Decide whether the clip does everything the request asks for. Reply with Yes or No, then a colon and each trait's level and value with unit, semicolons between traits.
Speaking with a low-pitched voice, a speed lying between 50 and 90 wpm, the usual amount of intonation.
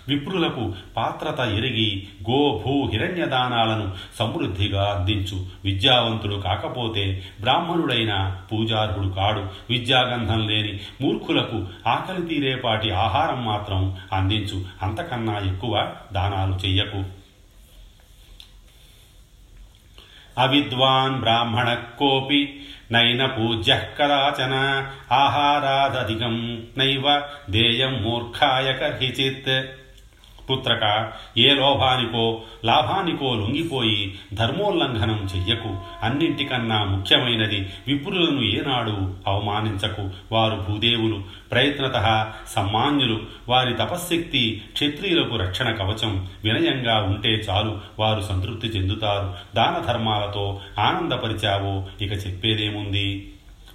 Yes: low, 110 Hz; slow, 70 wpm; average, 4.5 semitones